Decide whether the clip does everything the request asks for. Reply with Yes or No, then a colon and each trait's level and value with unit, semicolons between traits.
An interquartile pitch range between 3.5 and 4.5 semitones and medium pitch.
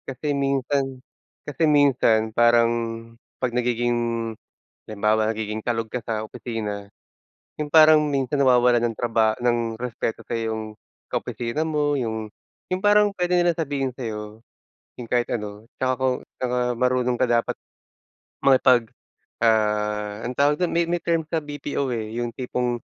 No: average, 3.8 semitones; low, 125 Hz